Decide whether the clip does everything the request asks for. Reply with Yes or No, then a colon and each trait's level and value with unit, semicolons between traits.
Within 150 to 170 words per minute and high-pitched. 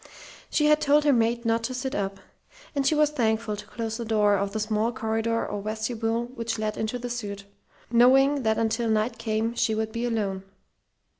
No: average, 200 wpm; high, 225 Hz